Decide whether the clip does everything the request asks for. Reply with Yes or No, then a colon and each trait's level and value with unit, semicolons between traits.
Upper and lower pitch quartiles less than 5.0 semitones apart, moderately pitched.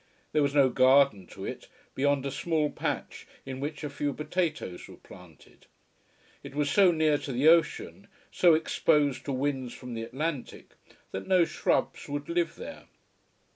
Yes: average, 3.3 semitones; medium, 145 Hz